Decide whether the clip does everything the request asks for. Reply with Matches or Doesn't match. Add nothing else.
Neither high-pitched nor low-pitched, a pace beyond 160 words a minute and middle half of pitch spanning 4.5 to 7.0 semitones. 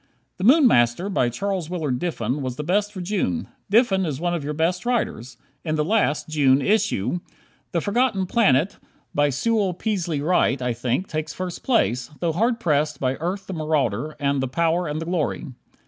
Matches